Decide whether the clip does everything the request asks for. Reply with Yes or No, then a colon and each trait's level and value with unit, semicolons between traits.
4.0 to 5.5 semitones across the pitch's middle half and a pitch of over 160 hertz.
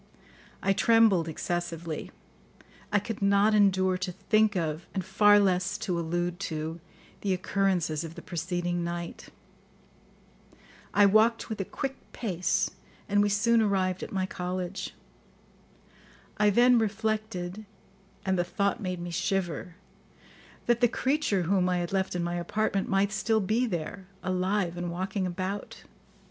No: average, 2.9 semitones; high, 190 Hz